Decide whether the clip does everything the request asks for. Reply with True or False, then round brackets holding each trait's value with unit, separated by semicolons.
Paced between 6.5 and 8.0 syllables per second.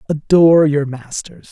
False (4.6 syllables/s)